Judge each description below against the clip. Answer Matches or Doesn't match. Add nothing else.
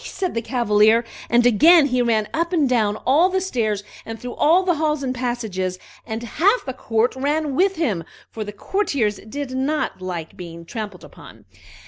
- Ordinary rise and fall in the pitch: Doesn't match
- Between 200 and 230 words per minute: Doesn't match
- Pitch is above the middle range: Matches